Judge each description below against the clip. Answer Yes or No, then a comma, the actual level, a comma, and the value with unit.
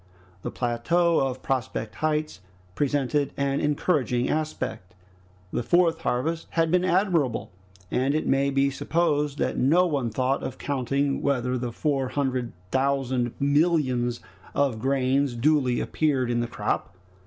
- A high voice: No, medium, 140 Hz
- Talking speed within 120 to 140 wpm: Yes, slow, 135 wpm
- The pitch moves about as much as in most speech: Yes, average, 3.3 semitones